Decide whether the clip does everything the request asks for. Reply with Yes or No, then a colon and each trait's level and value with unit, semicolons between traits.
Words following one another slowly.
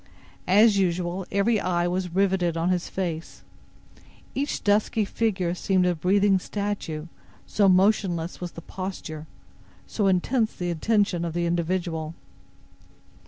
Yes: slow, 125 wpm